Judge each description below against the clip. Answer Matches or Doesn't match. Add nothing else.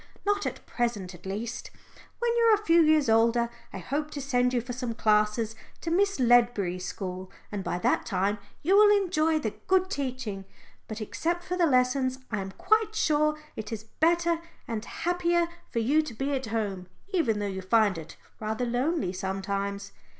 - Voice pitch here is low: Doesn't match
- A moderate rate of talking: Matches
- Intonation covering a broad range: Matches